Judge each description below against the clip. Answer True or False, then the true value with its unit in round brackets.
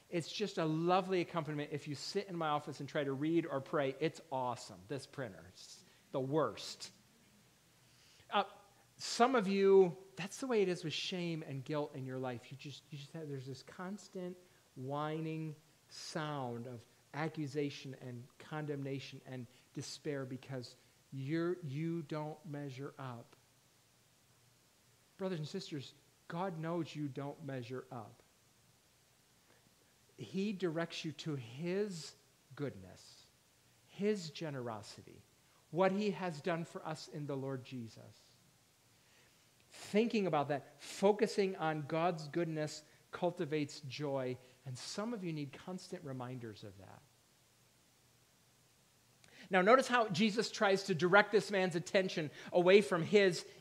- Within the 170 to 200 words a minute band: False (135 wpm)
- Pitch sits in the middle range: True (150 Hz)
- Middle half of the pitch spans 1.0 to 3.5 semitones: False (5.3 semitones)